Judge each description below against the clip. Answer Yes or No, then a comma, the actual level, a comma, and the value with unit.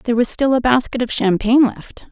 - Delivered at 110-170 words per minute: No, fast, 225 wpm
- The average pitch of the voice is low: No, high, 240 Hz